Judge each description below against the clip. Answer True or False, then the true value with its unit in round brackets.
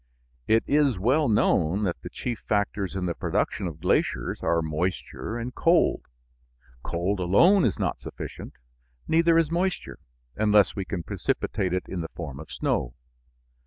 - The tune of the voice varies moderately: False (6.3 semitones)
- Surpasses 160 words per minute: False (155 wpm)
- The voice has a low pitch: True (100 Hz)